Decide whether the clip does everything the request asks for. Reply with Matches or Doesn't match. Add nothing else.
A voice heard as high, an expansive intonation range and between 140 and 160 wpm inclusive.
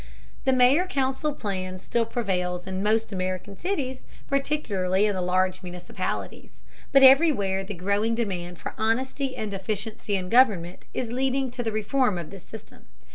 Matches